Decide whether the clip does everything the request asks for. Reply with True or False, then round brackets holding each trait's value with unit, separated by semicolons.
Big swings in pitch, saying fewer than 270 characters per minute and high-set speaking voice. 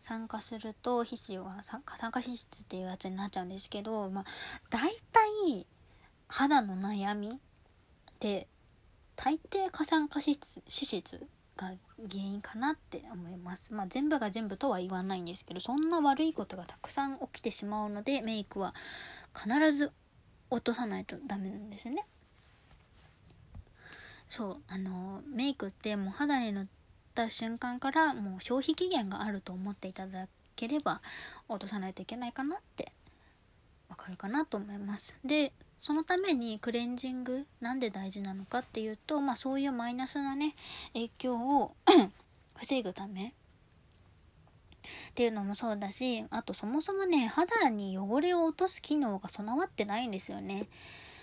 True (5.8 semitones; 255 characters per minute; 235 Hz)